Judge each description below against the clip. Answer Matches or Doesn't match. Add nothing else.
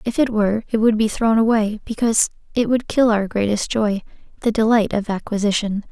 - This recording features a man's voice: Doesn't match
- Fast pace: Doesn't match